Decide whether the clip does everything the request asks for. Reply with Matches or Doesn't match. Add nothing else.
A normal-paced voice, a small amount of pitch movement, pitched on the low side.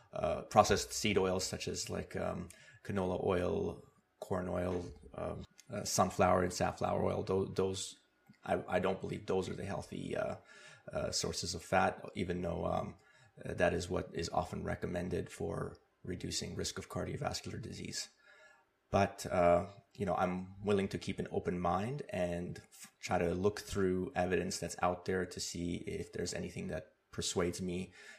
Matches